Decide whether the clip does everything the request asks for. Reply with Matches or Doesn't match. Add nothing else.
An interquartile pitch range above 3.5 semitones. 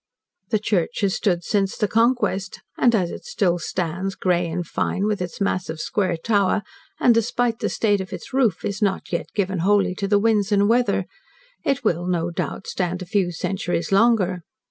Doesn't match